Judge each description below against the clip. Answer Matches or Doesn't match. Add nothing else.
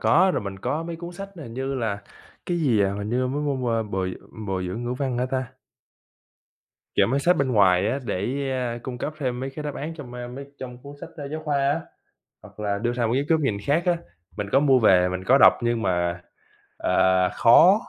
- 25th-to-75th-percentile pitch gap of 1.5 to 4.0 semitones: Doesn't match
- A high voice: Doesn't match